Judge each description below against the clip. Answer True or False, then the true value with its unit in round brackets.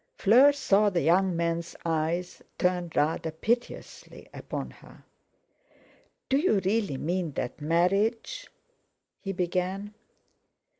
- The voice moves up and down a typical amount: True (3.6 semitones)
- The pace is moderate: False (105 wpm)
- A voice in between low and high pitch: True (180 Hz)